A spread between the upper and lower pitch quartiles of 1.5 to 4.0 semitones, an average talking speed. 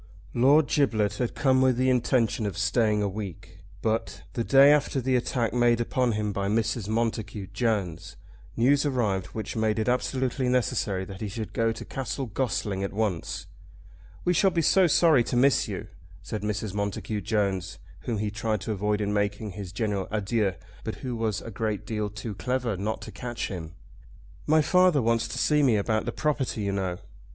Yes: average, 3.5 semitones; average, 185 wpm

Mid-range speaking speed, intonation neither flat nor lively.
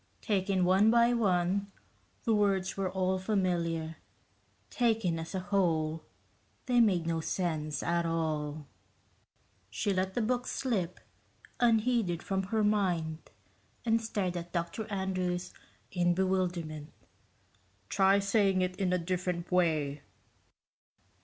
No: slow, 120 wpm; average, 3.0 semitones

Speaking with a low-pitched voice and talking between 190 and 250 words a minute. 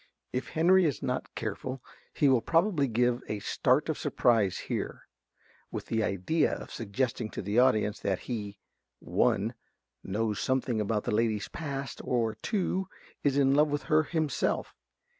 No: low, 125 Hz; average, 155 wpm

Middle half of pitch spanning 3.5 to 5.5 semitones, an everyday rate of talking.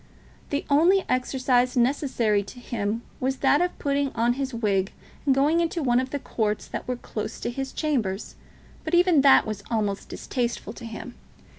Yes: average, 3.8 semitones; average, 175 wpm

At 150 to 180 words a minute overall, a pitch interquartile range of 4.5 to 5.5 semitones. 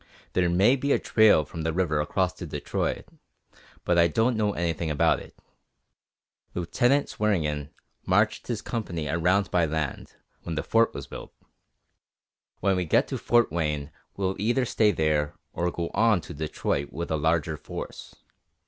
Yes: average, 160 wpm; average, 4.8 semitones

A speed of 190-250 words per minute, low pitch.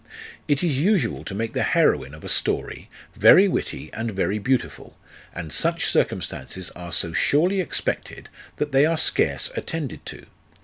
No: average, 160 wpm; low, 130 Hz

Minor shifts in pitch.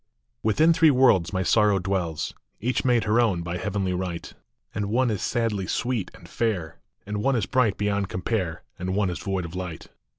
No: average, 4.0 semitones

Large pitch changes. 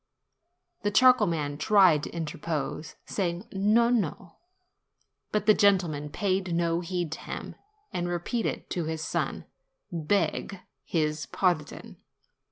No: average, 4.0 semitones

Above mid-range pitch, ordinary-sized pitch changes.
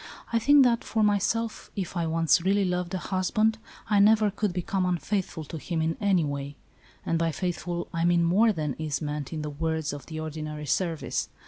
No: medium, 175 Hz; average, 4.2 semitones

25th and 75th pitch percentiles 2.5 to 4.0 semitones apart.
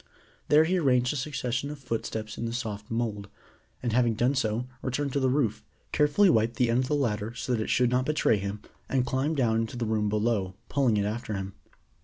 Yes: average, 3.4 semitones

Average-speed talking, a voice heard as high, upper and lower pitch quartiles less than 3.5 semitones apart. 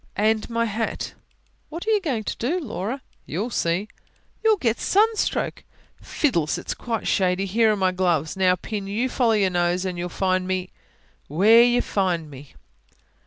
No: average, 165 wpm; high, 205 Hz; average, 4.6 semitones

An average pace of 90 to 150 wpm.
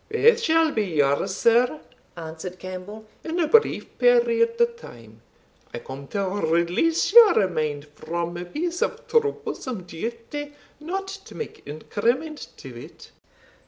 Yes: slow, 135 wpm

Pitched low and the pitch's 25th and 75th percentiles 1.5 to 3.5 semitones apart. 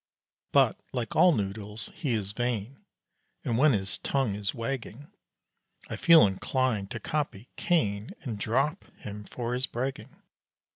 No: low, 120 Hz; average, 4.8 semitones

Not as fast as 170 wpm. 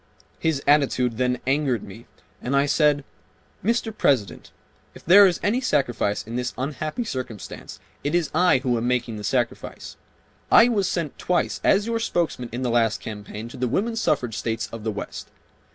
No: average, 175 wpm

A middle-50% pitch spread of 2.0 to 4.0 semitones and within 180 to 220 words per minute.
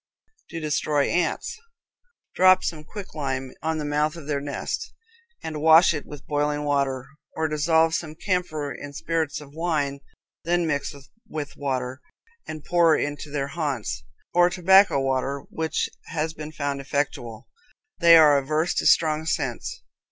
No: narrow, 2.4 semitones; average, 145 wpm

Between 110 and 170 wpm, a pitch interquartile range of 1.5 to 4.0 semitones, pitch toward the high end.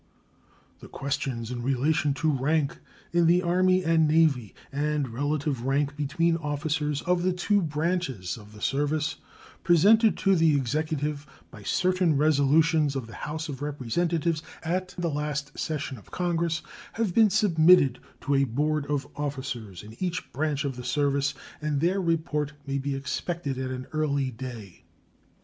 No: average, 155 wpm; average, 3.4 semitones; medium, 150 Hz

